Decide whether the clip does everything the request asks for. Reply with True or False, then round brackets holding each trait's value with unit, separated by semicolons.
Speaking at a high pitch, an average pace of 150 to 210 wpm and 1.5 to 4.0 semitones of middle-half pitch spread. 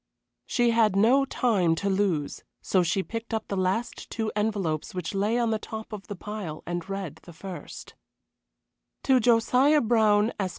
True (210 Hz; 170 wpm; 3.5 semitones)